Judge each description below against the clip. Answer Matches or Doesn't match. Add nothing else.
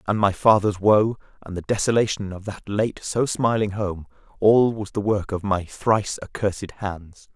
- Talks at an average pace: Matches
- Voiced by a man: Matches